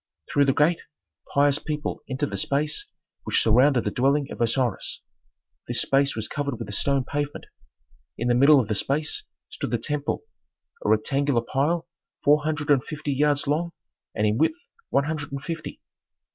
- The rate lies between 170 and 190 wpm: Yes, average, 175 wpm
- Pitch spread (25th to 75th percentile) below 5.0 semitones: Yes, average, 2.8 semitones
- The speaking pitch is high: No, medium, 140 Hz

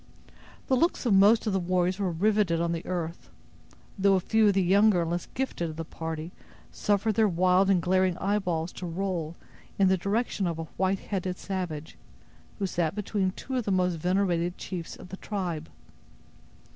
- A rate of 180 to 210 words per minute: Yes, average, 185 wpm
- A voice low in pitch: No, medium, 185 Hz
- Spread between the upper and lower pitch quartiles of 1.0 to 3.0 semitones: Yes, average, 2.7 semitones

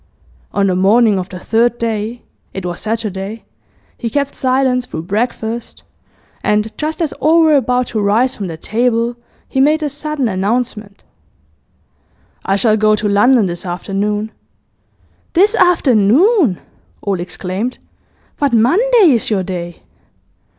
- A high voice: Yes, high, 225 Hz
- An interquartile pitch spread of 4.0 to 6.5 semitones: Yes, average, 4.6 semitones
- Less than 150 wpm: Yes, slow, 135 wpm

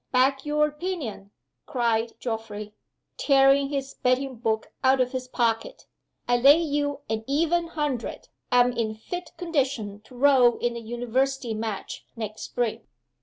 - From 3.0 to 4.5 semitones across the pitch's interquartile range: Yes, average, 3.8 semitones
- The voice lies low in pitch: No, very high, 255 Hz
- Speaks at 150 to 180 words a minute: No, average, 140 wpm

